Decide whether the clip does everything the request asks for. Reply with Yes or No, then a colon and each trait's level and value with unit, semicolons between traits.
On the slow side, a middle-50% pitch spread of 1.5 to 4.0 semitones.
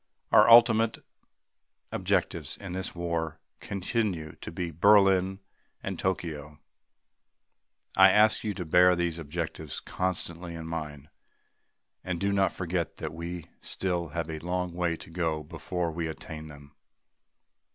Yes: slow, 130 wpm; average, 2.7 semitones